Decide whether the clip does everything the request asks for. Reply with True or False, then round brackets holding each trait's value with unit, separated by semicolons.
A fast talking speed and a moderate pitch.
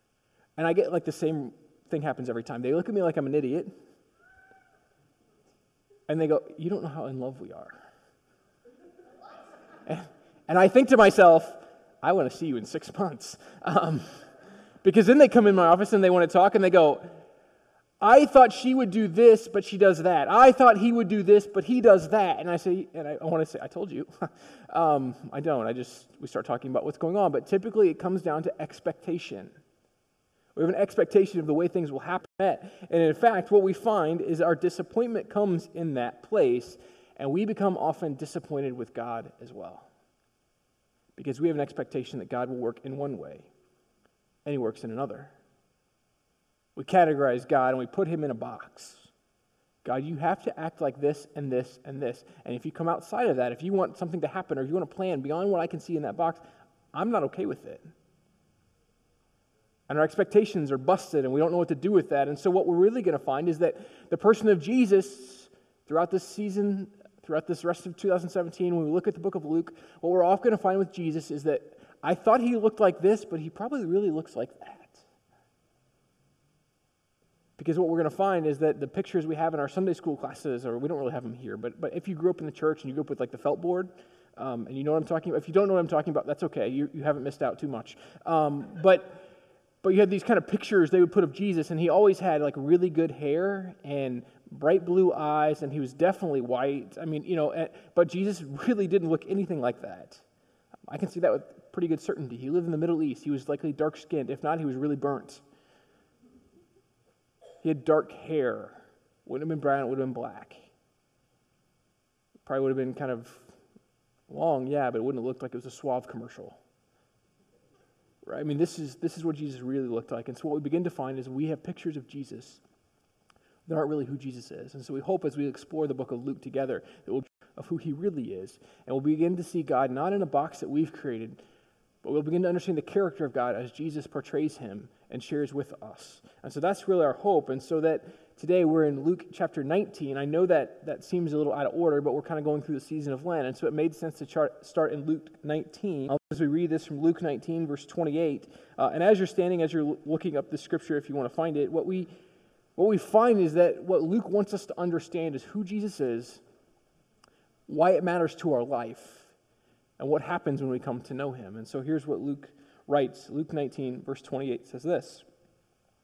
True (230 wpm; 160 Hz)